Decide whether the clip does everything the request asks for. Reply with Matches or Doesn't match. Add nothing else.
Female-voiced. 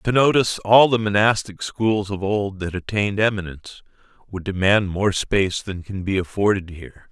Doesn't match